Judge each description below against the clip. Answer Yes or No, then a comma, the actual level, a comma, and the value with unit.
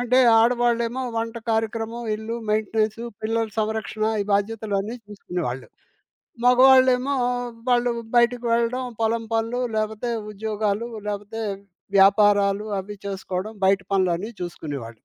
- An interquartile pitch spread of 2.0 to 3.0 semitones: Yes, average, 2.7 semitones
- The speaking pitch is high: Yes, high, 220 Hz